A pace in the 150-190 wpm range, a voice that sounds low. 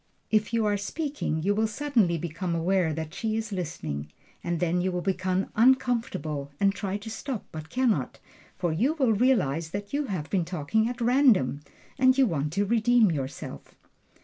No: average, 180 wpm; high, 200 Hz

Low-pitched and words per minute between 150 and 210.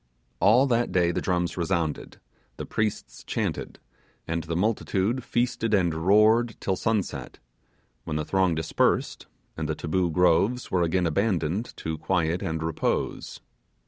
No: very low, 90 Hz; average, 140 wpm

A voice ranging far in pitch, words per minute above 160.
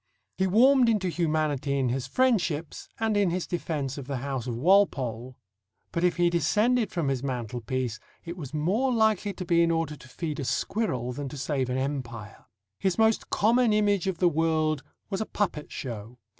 Yes: wide, 6.8 semitones; average, 185 wpm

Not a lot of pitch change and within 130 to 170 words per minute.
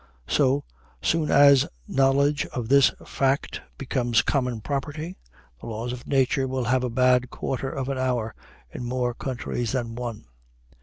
Yes: narrow, 2.1 semitones; average, 150 wpm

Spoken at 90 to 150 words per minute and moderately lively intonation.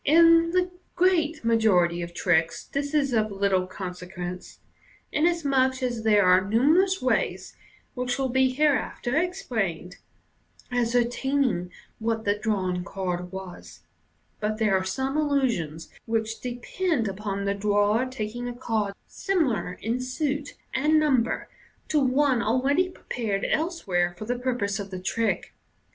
No: slow, 135 wpm; wide, 6.1 semitones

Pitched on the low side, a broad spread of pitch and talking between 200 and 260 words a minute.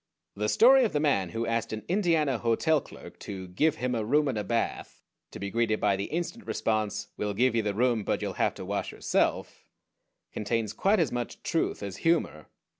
Yes: low, 115 Hz; wide, 6.2 semitones; fast, 205 wpm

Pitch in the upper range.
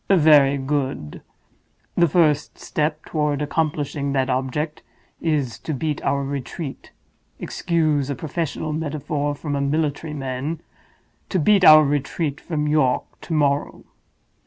No: medium, 150 Hz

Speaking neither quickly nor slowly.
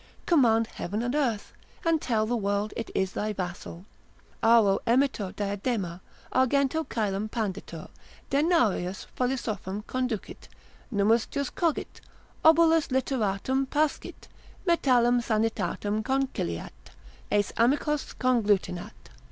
No: slow, 105 wpm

